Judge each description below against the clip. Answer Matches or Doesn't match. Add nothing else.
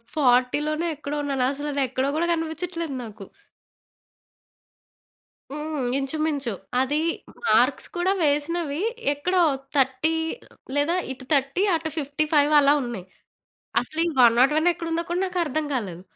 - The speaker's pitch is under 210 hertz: Doesn't match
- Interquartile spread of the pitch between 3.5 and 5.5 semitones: Doesn't match